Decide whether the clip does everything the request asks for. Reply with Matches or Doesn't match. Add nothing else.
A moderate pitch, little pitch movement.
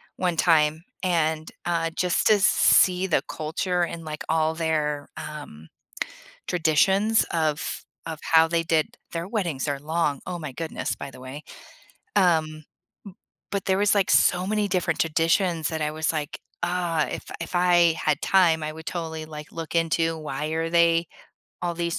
Matches